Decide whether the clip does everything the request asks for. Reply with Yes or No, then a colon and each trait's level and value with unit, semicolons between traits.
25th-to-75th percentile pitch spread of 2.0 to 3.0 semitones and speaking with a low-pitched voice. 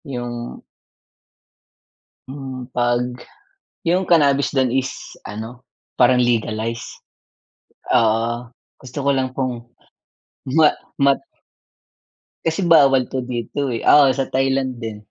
Yes: narrow, 2.4 semitones; low, 130 Hz